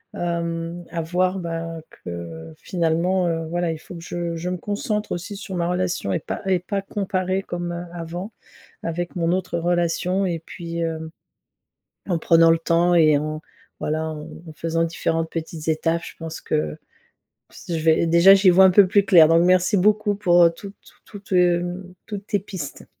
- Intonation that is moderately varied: No, narrow, 2.0 semitones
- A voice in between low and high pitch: Yes, medium, 170 Hz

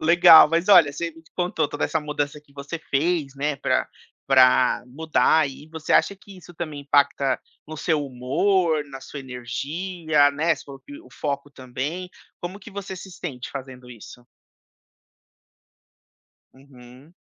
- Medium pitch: Yes, medium, 150 Hz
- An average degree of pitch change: Yes, average, 3.8 semitones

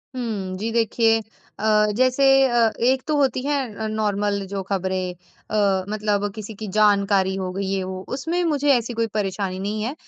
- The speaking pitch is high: Yes, high, 215 Hz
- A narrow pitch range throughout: No, average, 3.4 semitones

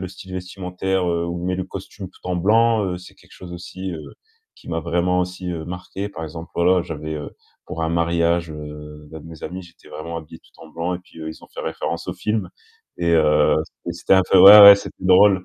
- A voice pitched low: Yes, very low, 85 Hz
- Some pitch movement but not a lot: No, narrow, 2.1 semitones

